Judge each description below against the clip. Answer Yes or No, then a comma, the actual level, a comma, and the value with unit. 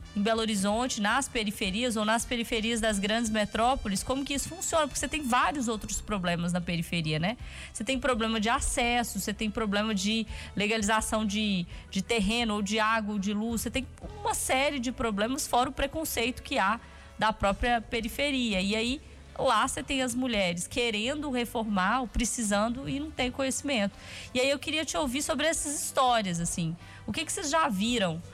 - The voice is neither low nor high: No, high, 230 Hz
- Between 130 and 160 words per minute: No, fast, 185 wpm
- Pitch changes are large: No, average, 3.7 semitones